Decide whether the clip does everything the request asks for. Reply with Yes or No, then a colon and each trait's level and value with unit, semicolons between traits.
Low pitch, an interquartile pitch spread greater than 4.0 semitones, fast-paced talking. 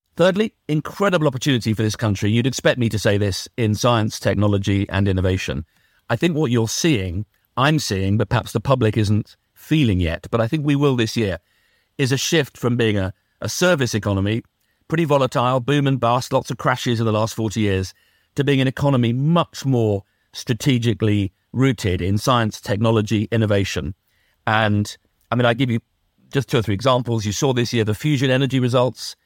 No: low, 115 Hz; average, 4.4 semitones; average, 185 wpm